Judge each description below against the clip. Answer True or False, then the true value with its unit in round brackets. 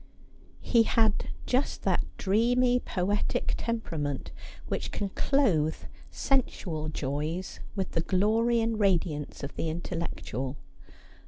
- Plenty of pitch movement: True (6.6 semitones)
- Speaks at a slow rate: True (105 wpm)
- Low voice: False (190 Hz)